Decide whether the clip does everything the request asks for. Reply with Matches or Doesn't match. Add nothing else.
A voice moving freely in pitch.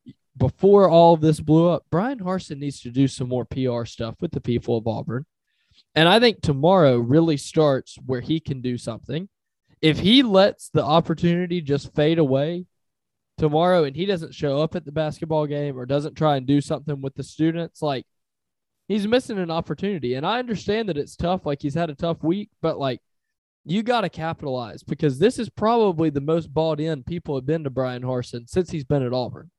Doesn't match